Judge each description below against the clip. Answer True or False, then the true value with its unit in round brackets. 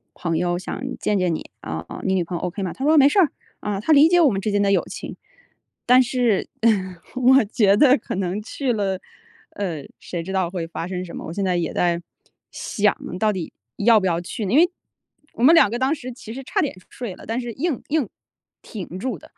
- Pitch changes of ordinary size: False (5.7 semitones)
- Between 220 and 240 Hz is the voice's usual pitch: False (205 Hz)